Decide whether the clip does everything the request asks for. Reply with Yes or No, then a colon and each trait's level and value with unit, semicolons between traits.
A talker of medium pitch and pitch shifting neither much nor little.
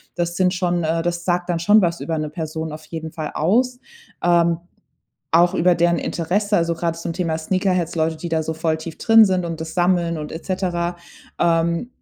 No: medium, 170 Hz; narrow, 1.8 semitones